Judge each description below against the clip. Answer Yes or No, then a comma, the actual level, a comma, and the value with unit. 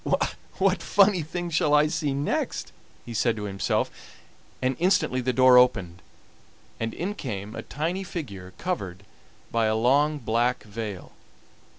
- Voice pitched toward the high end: No, low, 130 Hz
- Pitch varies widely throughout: Yes, wide, 6.8 semitones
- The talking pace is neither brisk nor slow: Yes, average, 145 wpm